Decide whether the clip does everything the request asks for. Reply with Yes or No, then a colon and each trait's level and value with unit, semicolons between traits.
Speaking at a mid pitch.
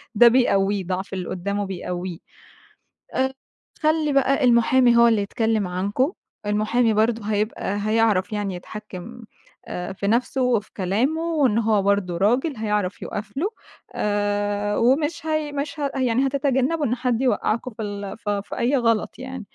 No: high, 225 Hz